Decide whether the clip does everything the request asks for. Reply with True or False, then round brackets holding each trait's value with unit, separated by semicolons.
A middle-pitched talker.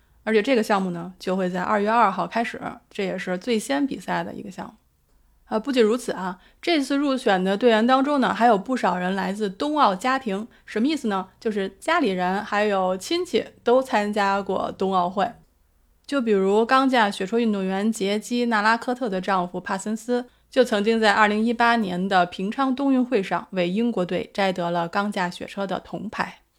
False (215 Hz)